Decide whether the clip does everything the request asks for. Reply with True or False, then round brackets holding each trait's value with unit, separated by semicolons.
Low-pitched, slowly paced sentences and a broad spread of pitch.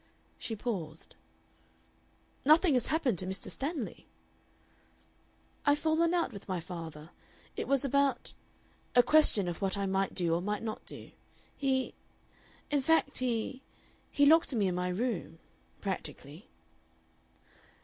False (225 Hz; 130 wpm; 7.2 semitones)